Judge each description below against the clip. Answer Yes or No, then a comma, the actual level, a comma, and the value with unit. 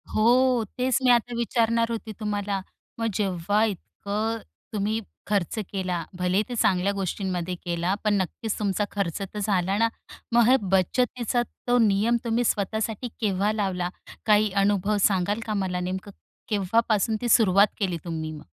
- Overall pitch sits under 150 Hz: No, high, 205 Hz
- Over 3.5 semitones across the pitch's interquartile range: No, average, 3.1 semitones